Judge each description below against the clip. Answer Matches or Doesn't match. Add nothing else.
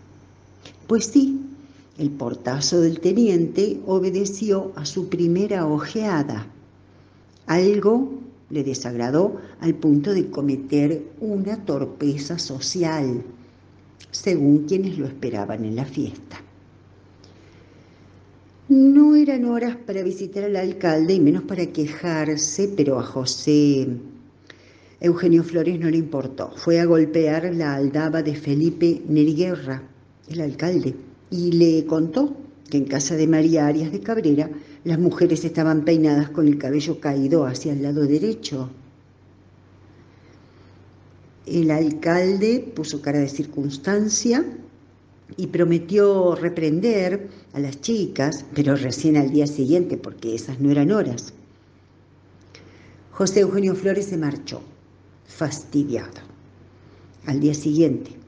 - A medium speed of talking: Doesn't match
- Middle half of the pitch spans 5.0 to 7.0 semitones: Matches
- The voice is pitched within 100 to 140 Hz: Doesn't match